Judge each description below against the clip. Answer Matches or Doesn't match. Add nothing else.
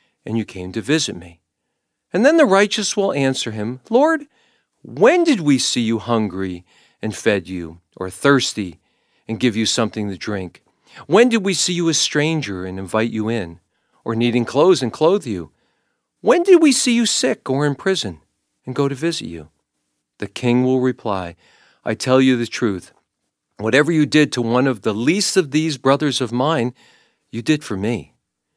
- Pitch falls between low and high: Doesn't match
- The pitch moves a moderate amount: Doesn't match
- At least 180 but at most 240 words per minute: Matches